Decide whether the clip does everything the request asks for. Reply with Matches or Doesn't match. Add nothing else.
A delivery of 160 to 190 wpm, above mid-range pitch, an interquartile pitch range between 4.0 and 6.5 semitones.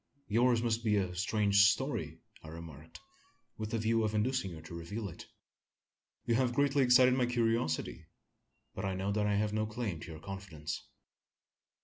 Doesn't match